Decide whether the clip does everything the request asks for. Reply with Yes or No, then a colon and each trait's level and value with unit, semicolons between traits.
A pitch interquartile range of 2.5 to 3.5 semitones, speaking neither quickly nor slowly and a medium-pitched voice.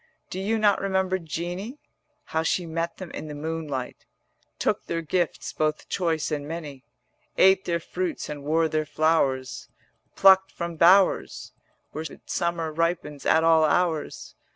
Yes: average, 3.0 semitones; average, 150 wpm; medium, 165 Hz